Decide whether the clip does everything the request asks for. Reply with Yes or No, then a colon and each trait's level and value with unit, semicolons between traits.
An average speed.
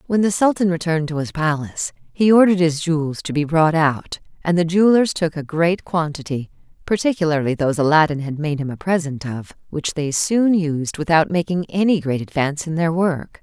Yes: average, 190 wpm